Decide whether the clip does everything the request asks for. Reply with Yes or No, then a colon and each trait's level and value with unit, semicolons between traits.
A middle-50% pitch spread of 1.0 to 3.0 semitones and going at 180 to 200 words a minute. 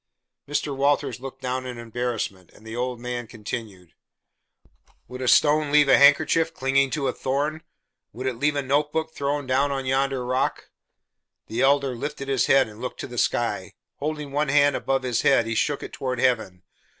Yes: average, 2.7 semitones; average, 185 wpm